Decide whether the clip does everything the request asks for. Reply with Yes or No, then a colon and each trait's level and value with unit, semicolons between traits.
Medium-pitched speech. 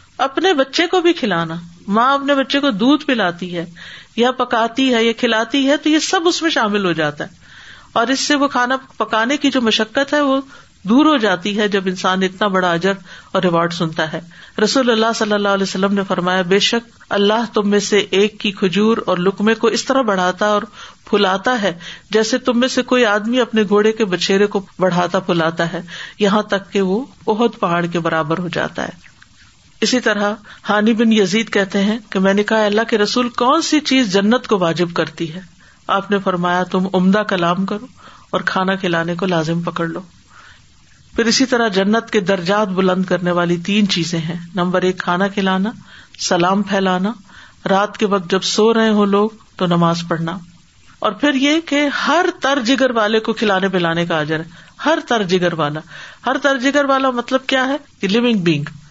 No: high, 205 Hz